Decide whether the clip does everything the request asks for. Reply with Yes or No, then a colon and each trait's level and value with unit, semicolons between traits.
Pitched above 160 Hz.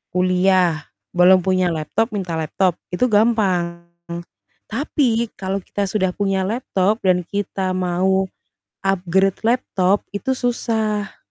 Yes: high, 190 Hz